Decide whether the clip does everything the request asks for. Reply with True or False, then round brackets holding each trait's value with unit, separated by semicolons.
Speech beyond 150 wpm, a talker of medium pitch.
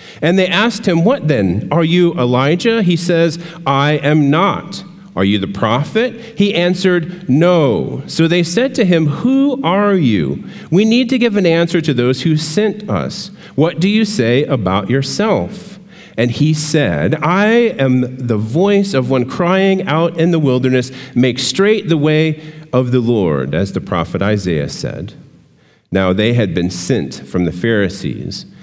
True (170 wpm; 165 Hz)